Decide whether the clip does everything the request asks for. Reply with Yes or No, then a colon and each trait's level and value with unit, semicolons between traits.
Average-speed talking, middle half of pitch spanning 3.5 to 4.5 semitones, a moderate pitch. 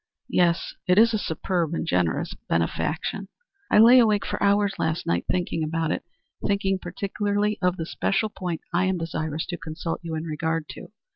Yes: average, 180 wpm; average, 3.8 semitones; medium, 175 Hz